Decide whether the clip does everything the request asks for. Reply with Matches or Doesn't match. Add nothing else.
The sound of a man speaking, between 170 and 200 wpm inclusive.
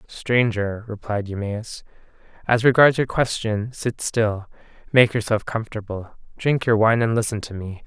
Doesn't match